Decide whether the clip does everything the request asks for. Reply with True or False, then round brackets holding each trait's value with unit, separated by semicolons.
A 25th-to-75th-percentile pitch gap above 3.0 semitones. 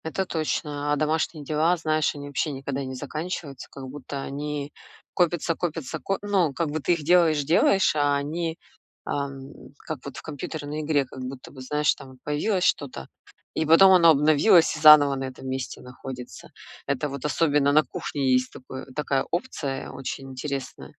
False (2.7 semitones)